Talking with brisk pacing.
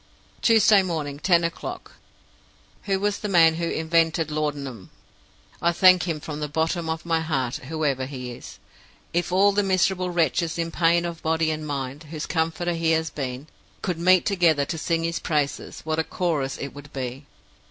No: average, 175 wpm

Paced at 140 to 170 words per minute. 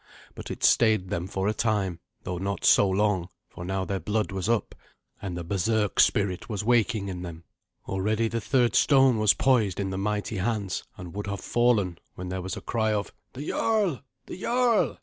No: average, 195 wpm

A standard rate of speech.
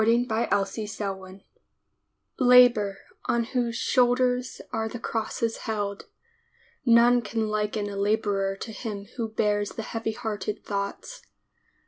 No: slow, 115 wpm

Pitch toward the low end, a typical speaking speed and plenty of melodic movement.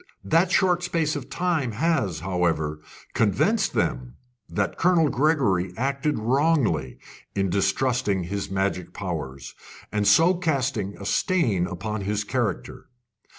No: low, 105 Hz; slow, 120 wpm; wide, 8.4 semitones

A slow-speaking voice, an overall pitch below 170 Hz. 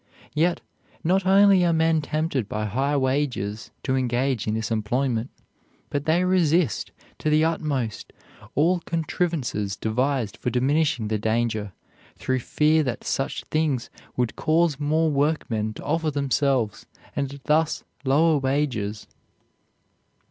Yes: slow, 125 wpm; medium, 140 Hz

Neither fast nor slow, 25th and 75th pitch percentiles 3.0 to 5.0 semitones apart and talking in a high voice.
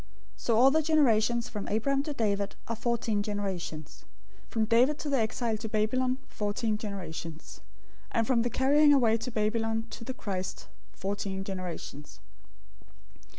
Yes: average, 150 wpm; average, 3.5 semitones; high, 225 Hz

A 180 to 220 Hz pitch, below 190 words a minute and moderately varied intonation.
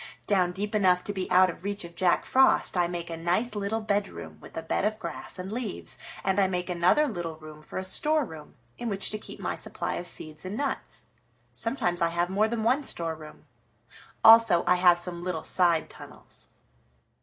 No: medium, 185 Hz; average, 200 wpm; average, 3.6 semitones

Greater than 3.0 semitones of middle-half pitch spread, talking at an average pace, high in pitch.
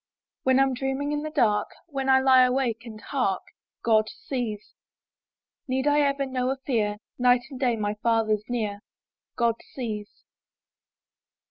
Yes: average, 3.6 semitones; average, 150 wpm; very high, 250 Hz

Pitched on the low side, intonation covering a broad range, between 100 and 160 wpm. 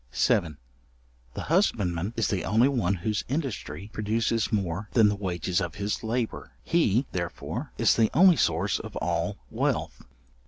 No: low, 105 Hz; average, 4.4 semitones; average, 150 wpm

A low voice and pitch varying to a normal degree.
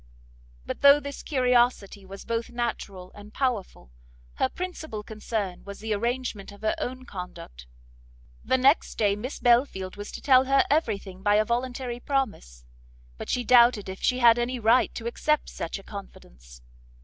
No: high, 230 Hz; average, 4.2 semitones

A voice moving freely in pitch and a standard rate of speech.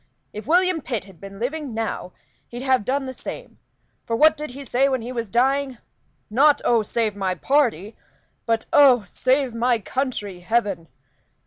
No: average, 4.4 semitones; average, 165 wpm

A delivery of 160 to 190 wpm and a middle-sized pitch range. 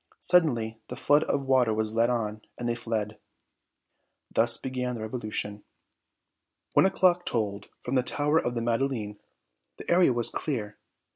No: average, 150 wpm; average, 3.6 semitones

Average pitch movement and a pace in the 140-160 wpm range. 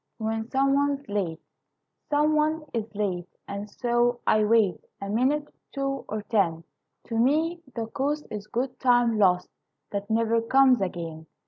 Yes: average, 5.0 semitones; average, 150 wpm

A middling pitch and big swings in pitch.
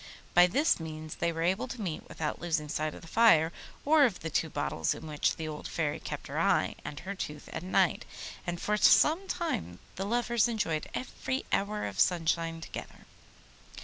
Yes: medium, 170 Hz; wide, 6.0 semitones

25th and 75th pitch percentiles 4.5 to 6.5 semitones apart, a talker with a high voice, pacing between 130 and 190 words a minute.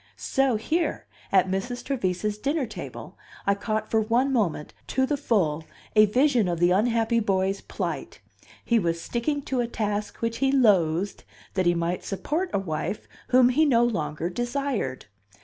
Yes: average, 5.2 semitones; high, 215 Hz; average, 165 wpm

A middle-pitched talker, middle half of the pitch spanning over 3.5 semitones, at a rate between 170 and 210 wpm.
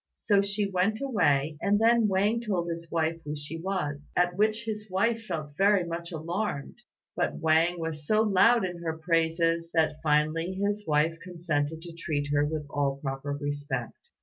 Yes: medium, 170 Hz; average, 4.7 semitones; average, 175 wpm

